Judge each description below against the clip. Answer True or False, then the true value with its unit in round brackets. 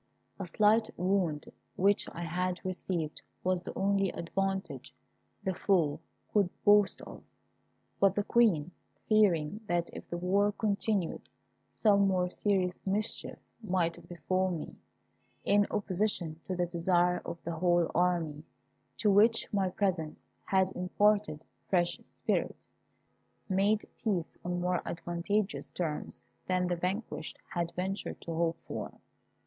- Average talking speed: False (130 wpm)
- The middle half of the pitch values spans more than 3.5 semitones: False (2.7 semitones)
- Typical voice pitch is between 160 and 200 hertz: True (185 Hz)